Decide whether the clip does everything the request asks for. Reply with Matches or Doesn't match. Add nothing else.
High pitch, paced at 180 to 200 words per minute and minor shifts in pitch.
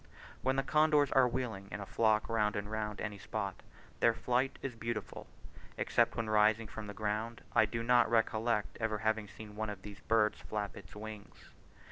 Doesn't match